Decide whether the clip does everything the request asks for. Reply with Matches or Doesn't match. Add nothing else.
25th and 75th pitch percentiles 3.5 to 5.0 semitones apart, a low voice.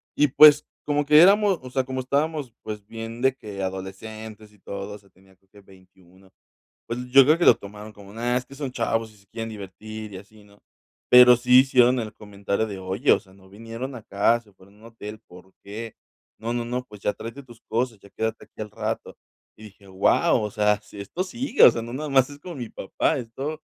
Matches